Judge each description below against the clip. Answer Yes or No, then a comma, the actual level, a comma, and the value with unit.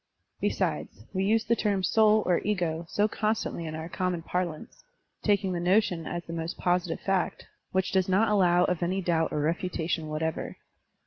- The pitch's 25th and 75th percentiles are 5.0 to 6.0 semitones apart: No, average, 2.9 semitones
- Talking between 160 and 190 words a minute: Yes, average, 175 wpm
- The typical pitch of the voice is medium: Yes, medium, 180 Hz